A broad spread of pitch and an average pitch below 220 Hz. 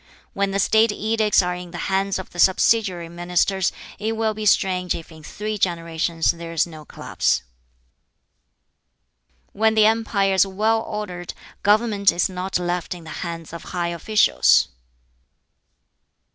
No: average, 3.5 semitones; high, 190 Hz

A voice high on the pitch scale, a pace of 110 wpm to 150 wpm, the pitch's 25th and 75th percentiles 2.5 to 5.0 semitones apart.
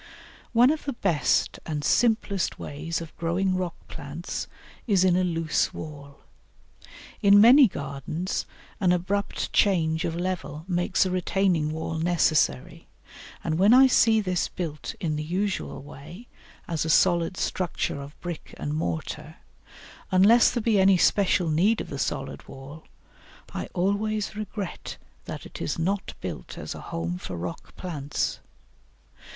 No: medium, 175 Hz; average, 145 wpm; average, 4.2 semitones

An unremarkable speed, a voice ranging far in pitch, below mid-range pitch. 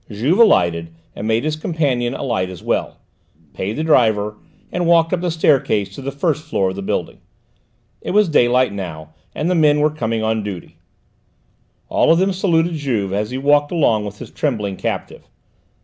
Yes: average, 180 wpm; wide, 7.4 semitones; low, 130 Hz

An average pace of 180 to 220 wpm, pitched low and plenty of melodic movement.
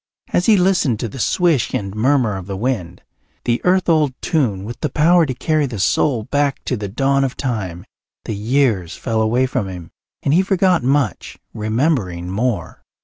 Yes: average, 185 wpm; low, 125 Hz; wide, 5.7 semitones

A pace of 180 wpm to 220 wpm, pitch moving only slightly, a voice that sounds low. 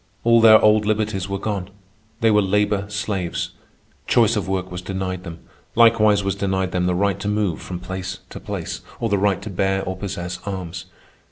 Yes: average, 190 wpm; narrow, 2.1 semitones; low, 100 Hz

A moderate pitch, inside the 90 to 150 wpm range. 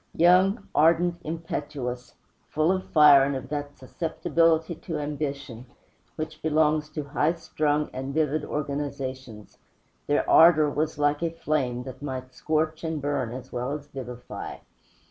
Yes: medium, 150 Hz; average, 140 wpm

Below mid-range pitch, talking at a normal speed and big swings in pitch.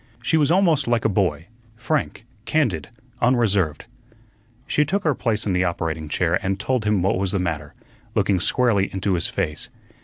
Yes: low, 100 Hz; average, 175 wpm; wide, 6.0 semitones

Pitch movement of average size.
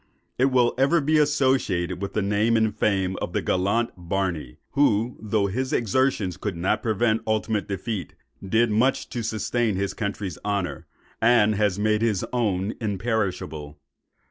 Yes: average, 3.4 semitones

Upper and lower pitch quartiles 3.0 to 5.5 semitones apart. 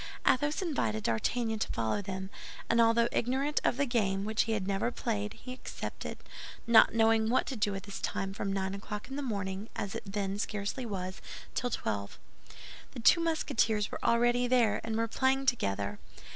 Yes: average, 3.9 semitones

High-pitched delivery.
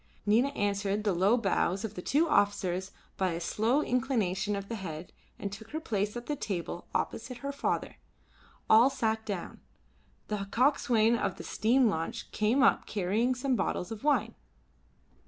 Yes: high, 215 Hz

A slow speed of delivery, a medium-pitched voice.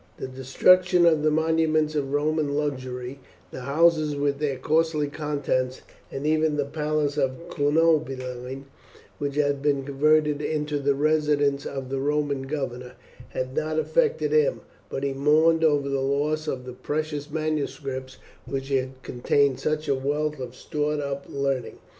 No: average, 150 wpm; medium, 145 Hz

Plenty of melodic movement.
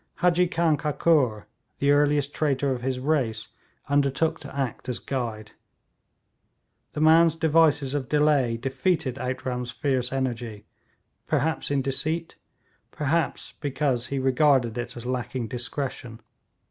No: average, 3.3 semitones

